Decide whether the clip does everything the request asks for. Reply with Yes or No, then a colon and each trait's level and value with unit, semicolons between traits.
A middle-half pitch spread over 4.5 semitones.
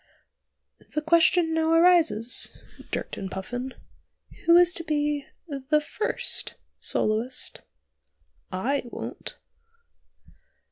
Yes: average, 5.0 semitones